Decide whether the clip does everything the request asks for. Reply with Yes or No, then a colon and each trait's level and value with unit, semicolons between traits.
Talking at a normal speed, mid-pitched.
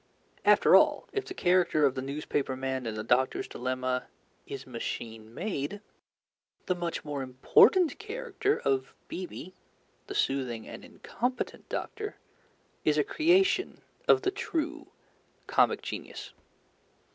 No: slow, 125 wpm; medium, 150 Hz